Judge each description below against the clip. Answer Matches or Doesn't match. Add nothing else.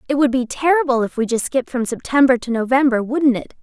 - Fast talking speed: Matches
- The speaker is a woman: Matches